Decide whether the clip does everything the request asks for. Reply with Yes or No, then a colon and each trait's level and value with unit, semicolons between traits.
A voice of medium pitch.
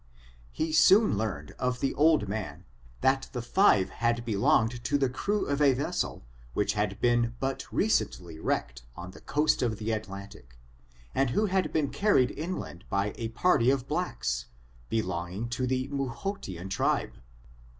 No: low, 120 Hz